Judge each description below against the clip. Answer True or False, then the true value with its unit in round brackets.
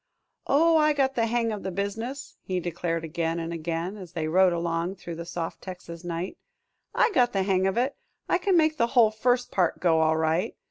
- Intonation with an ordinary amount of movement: False (6.2 semitones)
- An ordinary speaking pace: False (215 wpm)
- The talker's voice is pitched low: False (185 Hz)